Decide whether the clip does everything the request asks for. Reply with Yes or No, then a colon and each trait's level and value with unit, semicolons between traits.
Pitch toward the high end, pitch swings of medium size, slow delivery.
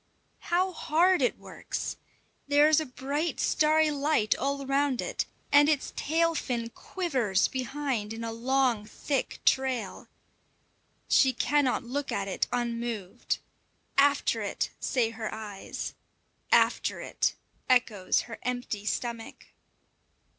Yes: very high, 260 Hz; average, 4.1 semitones; slow, 120 wpm